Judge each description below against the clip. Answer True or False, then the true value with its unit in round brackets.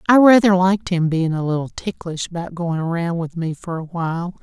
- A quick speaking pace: True (215 wpm)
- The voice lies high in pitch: False (175 Hz)